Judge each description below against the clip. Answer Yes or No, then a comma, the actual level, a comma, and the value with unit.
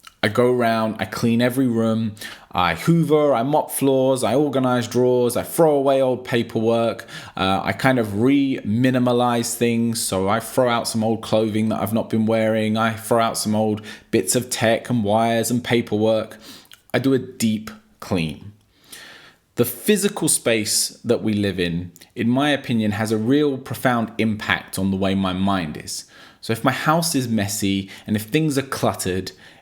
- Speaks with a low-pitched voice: Yes, low, 115 Hz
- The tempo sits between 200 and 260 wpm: No, average, 180 wpm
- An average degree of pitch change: Yes, average, 3.1 semitones